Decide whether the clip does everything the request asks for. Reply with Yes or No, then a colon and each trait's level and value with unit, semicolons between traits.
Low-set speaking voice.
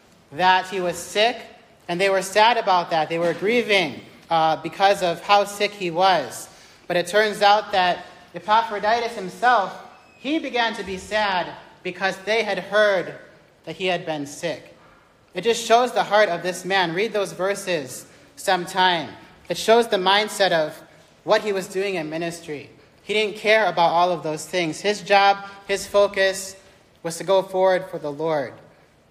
No: high, 190 Hz